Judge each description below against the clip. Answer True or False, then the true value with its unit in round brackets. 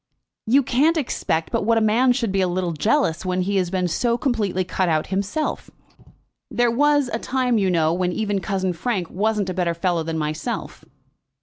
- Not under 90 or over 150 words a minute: False (195 wpm)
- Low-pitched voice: False (195 Hz)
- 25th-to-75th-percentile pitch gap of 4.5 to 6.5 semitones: True (5.1 semitones)